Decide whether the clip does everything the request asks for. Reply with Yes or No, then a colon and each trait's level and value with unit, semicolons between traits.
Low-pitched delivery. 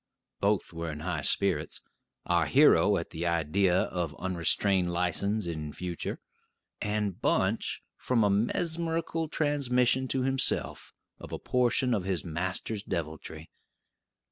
Yes: very low, 95 Hz